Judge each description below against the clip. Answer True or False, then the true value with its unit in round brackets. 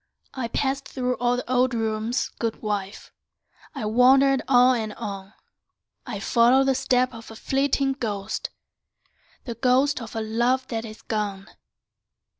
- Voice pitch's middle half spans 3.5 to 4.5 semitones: False (2.9 semitones)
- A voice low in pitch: False (240 Hz)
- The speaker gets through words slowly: False (145 wpm)